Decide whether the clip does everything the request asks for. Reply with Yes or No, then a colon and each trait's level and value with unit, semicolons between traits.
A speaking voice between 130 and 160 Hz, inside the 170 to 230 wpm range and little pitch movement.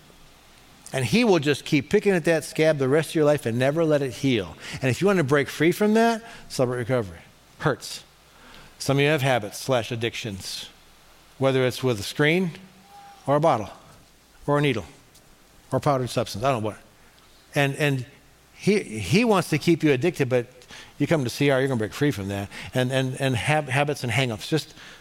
No: medium, 140 Hz; fast, 205 wpm; average, 3.9 semitones